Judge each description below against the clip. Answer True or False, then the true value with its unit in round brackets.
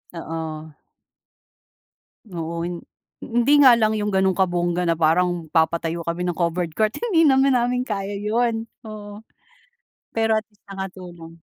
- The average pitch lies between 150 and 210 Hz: True (190 Hz)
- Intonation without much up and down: False (4.8 semitones)